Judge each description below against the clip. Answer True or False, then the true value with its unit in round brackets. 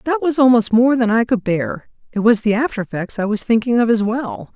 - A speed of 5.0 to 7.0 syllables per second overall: True (5.5 syllables/s)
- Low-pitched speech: False (225 Hz)